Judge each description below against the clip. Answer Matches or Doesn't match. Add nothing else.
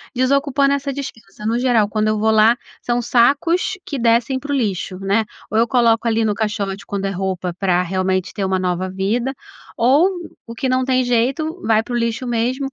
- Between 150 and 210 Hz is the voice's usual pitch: Doesn't match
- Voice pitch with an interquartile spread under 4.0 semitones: Doesn't match